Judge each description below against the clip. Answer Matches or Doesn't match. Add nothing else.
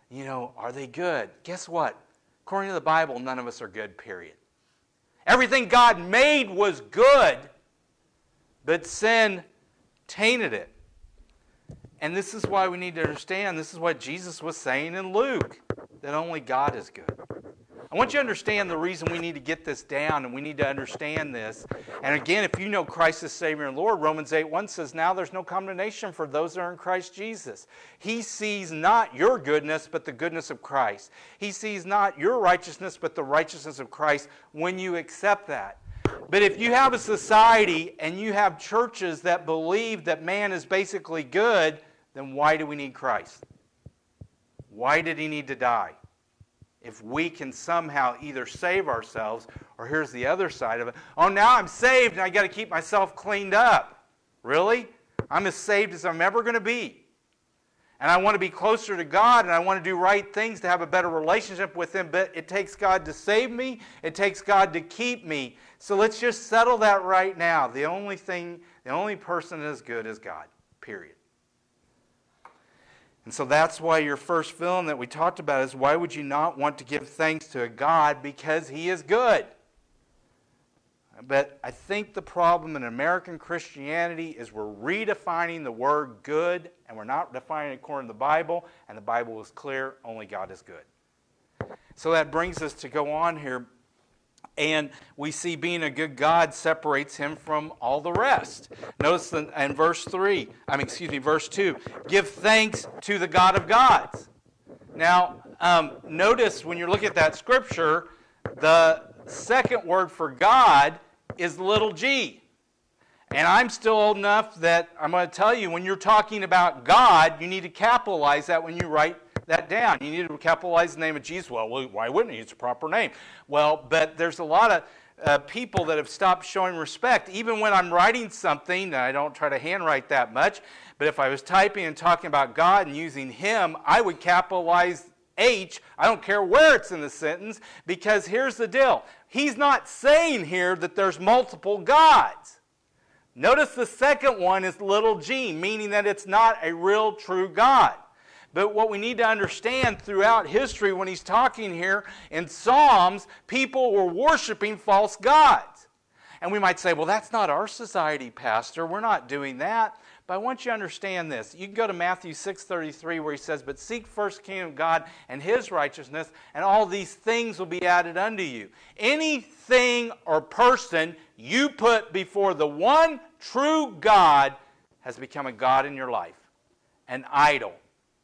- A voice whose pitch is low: Doesn't match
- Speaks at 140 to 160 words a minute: Doesn't match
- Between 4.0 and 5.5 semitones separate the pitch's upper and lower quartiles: Matches